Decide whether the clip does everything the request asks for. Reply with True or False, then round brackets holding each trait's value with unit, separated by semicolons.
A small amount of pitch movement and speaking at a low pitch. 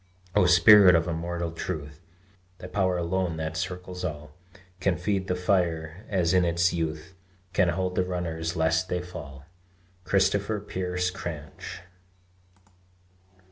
True (2.1 semitones; 90 Hz)